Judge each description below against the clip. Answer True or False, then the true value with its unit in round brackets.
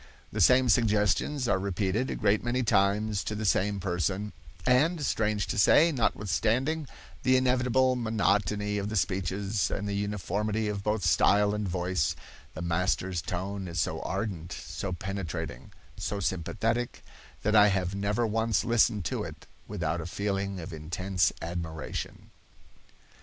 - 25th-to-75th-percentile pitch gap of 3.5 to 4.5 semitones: False (3.0 semitones)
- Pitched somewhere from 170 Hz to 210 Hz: False (100 Hz)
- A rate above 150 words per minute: False (145 wpm)